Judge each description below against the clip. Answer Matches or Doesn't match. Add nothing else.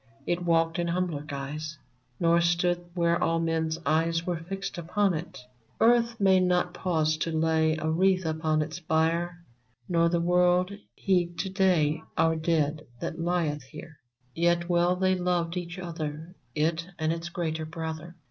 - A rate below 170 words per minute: Matches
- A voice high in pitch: Doesn't match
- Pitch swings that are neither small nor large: Doesn't match